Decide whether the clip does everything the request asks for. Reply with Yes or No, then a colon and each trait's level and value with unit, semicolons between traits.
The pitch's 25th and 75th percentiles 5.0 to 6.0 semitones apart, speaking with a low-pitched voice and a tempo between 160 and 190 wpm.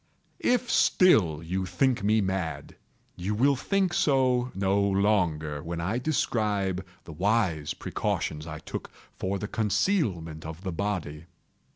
No: average, 5.3 semitones; very low, 95 Hz; slow, 135 wpm